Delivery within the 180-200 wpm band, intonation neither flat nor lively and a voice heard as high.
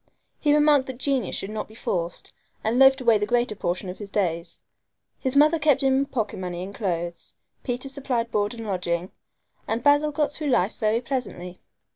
No: average, 190 wpm; wide, 6.1 semitones; high, 230 Hz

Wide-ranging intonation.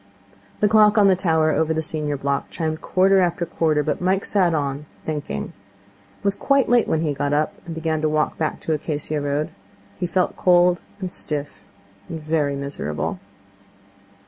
No: average, 3.4 semitones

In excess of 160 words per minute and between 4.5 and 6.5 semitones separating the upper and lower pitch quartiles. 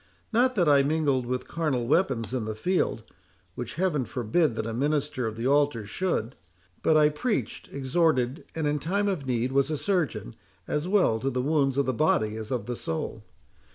Yes: average, 185 wpm; average, 5.3 semitones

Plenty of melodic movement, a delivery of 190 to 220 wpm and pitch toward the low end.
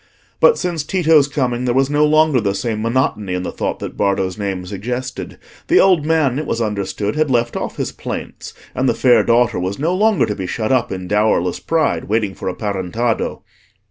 Yes: wide, 6.5 semitones; fast, 205 wpm; low, 120 Hz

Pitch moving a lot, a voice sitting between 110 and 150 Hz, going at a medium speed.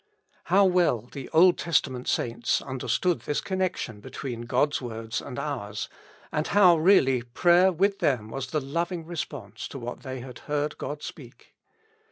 Yes: wide, 6.0 semitones; medium, 140 Hz; average, 155 wpm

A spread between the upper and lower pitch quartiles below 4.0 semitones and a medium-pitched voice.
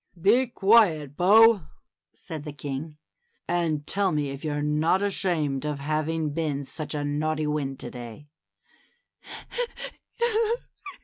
Yes: average, 3.1 semitones; medium, 155 Hz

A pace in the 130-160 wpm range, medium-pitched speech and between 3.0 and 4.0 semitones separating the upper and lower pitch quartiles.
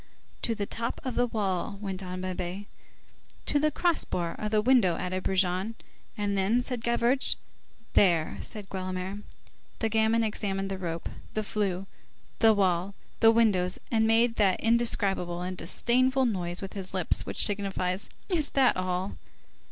No: average, 155 wpm; high, 200 Hz; average, 3.7 semitones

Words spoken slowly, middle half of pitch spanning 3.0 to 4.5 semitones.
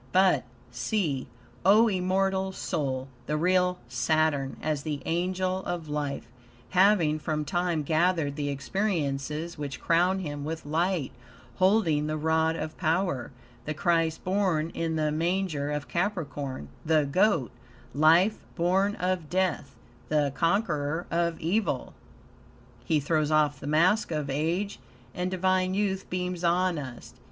Yes: slow, 130 wpm; average, 3.8 semitones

